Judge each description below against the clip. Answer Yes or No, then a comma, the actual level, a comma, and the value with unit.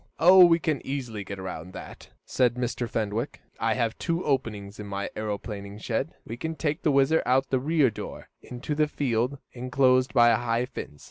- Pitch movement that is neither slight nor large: Yes, average, 4.5 semitones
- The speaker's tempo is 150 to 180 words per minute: No, average, 195 wpm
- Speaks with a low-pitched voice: Yes, low, 125 Hz